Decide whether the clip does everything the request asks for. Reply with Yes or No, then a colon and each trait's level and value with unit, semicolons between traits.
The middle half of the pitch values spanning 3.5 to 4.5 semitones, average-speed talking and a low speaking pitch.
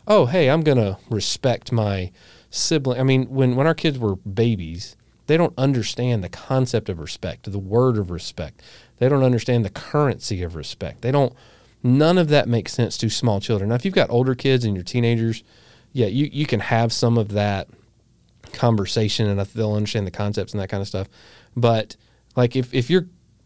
Yes: average, 3.9 semitones; average, 195 wpm; low, 115 Hz